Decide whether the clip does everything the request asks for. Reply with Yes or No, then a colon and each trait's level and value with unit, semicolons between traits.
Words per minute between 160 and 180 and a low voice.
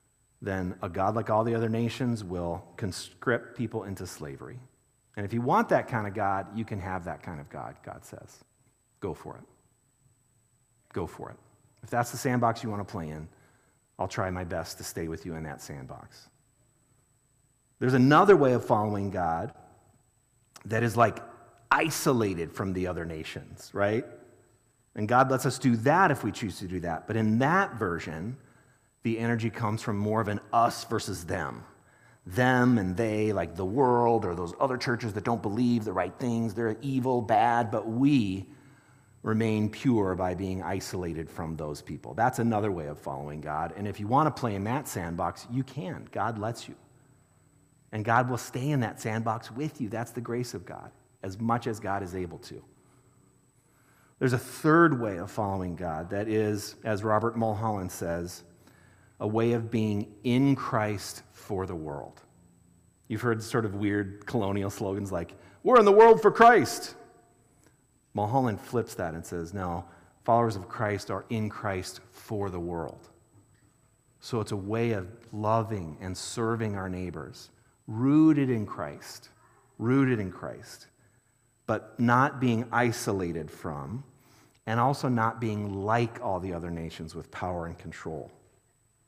Yes: average, 170 wpm; low, 110 Hz